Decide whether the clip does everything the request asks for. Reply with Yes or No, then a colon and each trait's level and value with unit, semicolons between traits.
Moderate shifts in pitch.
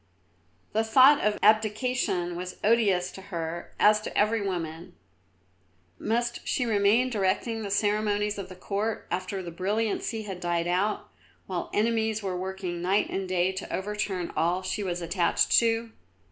Yes: average, 3.2 semitones